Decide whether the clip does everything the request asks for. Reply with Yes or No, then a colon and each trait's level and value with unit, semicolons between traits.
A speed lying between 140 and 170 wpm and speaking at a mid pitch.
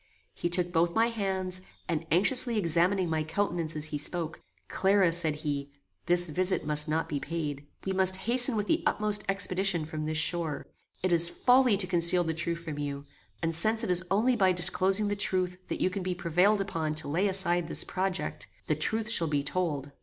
No: average, 200 wpm; medium, 175 Hz